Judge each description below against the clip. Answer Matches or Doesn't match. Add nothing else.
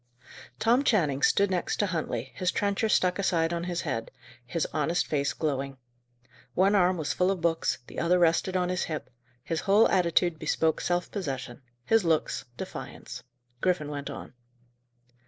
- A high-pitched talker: Doesn't match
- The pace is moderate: Matches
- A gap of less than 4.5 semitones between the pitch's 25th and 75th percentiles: Matches